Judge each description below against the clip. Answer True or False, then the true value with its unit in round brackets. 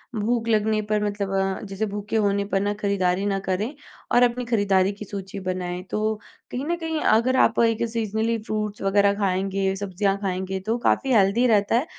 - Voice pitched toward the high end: True (205 Hz)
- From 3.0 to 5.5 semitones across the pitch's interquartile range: False (2.6 semitones)